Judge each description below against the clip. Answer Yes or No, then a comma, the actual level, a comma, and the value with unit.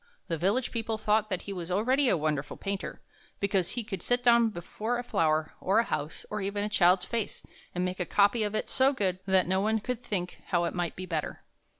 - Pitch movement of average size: Yes, average, 3.8 semitones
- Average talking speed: No, fast, 230 wpm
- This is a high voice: Yes, high, 200 Hz